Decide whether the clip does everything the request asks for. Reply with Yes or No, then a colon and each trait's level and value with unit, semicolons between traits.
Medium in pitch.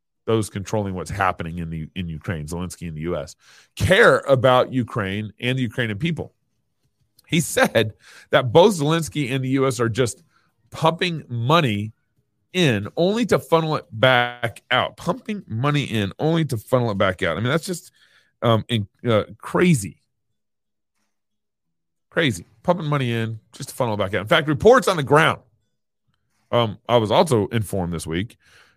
No: low, 115 Hz